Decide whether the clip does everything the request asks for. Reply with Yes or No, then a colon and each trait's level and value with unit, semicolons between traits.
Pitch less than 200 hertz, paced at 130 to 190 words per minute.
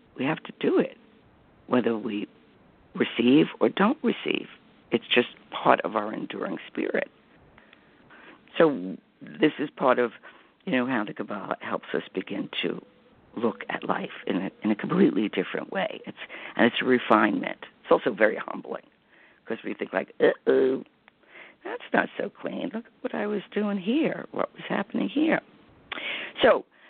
No: high, 225 Hz; average, 160 wpm